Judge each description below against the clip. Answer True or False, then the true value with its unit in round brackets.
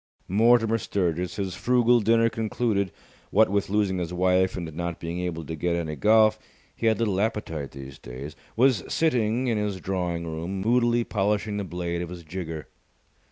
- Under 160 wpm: False (170 wpm)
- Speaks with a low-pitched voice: True (95 Hz)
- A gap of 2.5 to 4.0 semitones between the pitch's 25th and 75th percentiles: False (4.4 semitones)